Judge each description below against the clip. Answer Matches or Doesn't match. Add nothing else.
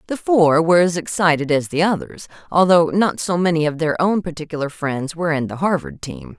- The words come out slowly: Doesn't match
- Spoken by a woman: Matches